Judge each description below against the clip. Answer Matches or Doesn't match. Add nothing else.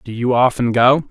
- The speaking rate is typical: Doesn't match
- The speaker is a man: Matches